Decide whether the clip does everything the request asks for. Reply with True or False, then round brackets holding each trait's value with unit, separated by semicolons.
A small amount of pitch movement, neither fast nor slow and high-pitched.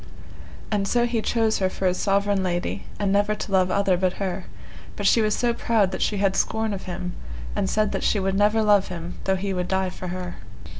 False (2.3 semitones; 230 wpm; 195 Hz)